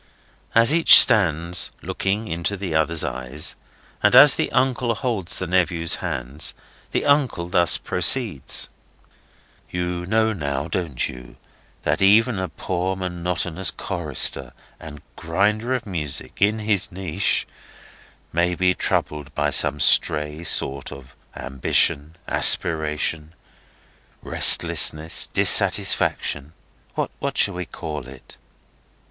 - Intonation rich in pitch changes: No, average, 4.3 semitones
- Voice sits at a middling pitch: No, very low, 85 Hz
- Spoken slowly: Yes, slow, 110 wpm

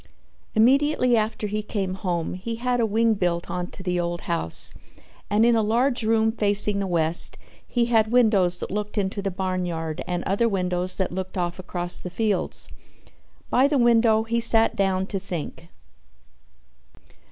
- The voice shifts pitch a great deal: No, average, 4.0 semitones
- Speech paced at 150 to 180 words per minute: Yes, average, 165 wpm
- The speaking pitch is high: Yes, high, 200 Hz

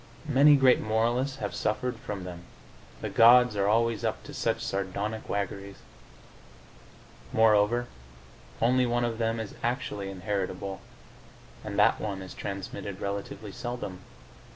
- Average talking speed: No, slow, 130 wpm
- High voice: No, low, 110 Hz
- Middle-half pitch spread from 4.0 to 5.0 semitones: No, average, 3.4 semitones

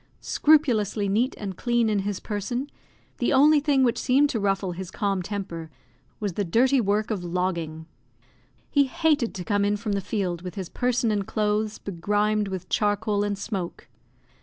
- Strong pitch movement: No, average, 3.6 semitones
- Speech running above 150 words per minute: Yes, average, 170 wpm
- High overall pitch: Yes, high, 205 Hz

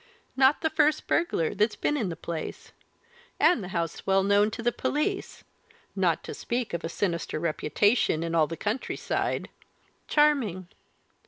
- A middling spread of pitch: No, wide, 7.9 semitones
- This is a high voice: Yes, high, 205 Hz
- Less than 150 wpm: No, average, 160 wpm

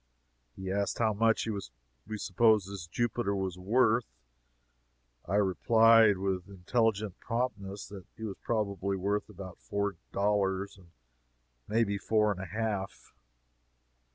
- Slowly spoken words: Yes, slow, 125 wpm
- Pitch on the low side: Yes, low, 100 Hz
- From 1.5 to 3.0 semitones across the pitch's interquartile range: Yes, narrow, 2.5 semitones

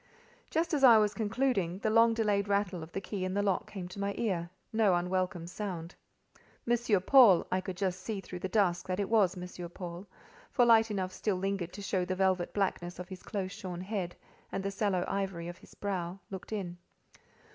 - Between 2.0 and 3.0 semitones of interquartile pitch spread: Yes, narrow, 2.5 semitones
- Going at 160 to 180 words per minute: No, average, 200 wpm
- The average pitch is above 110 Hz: Yes, high, 190 Hz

